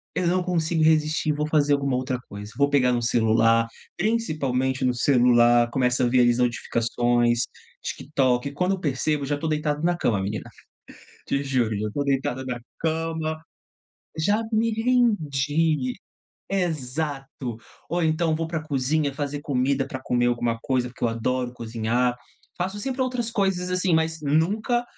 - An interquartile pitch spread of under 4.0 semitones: No, average, 4.7 semitones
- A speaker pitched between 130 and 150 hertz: Yes, medium, 140 Hz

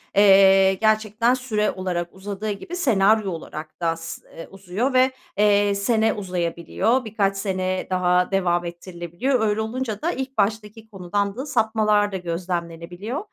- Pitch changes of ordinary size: Yes, average, 3.4 semitones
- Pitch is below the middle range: No, high, 200 Hz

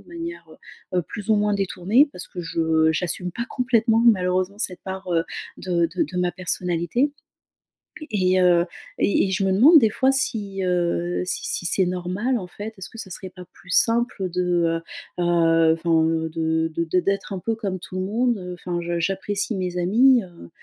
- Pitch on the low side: No, medium, 185 Hz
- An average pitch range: Yes, average, 3.3 semitones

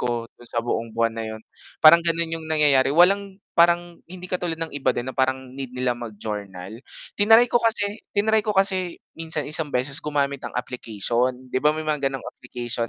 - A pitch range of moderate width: No, wide, 6.1 semitones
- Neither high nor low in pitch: Yes, medium, 145 Hz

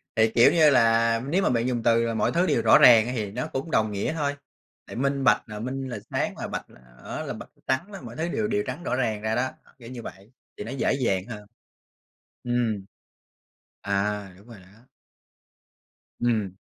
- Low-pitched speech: Yes, low, 120 Hz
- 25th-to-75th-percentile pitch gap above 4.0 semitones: No, average, 3.5 semitones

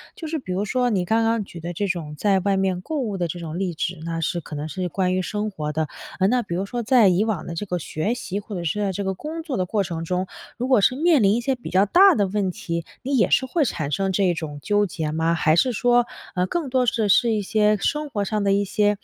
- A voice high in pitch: Yes, high, 200 Hz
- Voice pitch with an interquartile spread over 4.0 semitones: Yes, average, 4.7 semitones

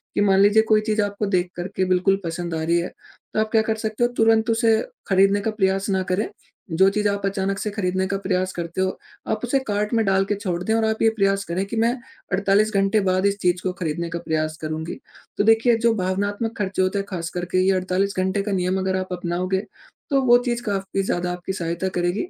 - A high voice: Yes, high, 195 Hz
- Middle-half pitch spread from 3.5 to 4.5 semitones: No, average, 2.7 semitones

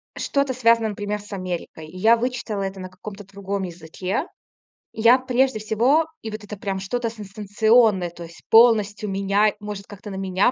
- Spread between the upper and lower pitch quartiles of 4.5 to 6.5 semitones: No, average, 2.9 semitones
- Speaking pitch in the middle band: No, high, 205 Hz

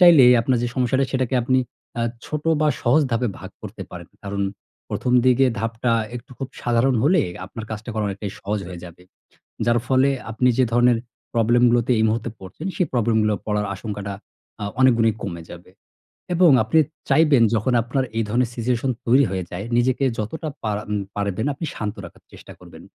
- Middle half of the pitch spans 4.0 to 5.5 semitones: No, average, 3.5 semitones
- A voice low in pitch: Yes, low, 120 Hz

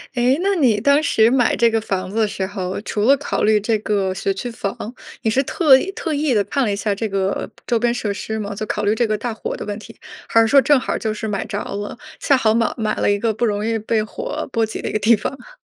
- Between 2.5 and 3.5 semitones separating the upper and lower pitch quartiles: Yes, average, 3.1 semitones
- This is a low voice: No, high, 220 Hz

